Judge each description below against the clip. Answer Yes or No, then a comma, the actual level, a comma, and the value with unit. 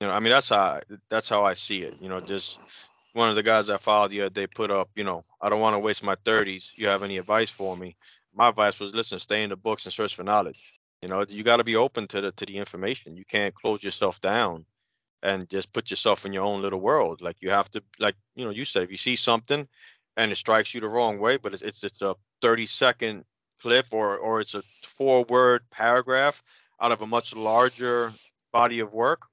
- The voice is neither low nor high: No, low, 105 Hz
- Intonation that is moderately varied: Yes, average, 3.1 semitones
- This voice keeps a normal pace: No, fast, 250 wpm